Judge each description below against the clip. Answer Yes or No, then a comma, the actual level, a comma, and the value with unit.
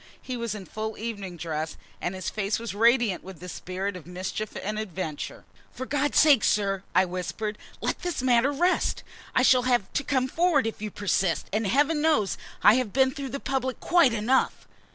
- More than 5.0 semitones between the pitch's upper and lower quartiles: Yes, wide, 5.4 semitones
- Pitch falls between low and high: No, high, 220 Hz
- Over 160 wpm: Yes, average, 195 wpm